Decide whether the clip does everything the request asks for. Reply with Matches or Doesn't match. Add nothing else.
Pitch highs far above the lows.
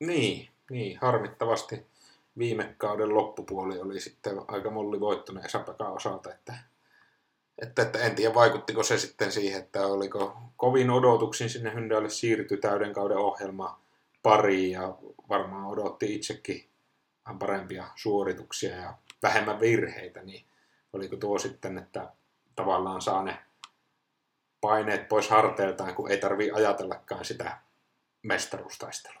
Doesn't match